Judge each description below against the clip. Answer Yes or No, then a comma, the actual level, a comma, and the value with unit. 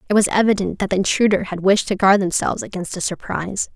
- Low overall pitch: No, high, 195 Hz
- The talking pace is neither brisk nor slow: No, fast, 225 wpm